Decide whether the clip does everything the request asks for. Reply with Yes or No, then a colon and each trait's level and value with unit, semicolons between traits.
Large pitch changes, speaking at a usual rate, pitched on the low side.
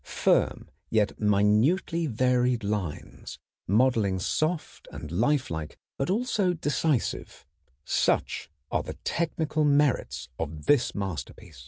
No: wide, 7.3 semitones; slow, 105 wpm; low, 125 Hz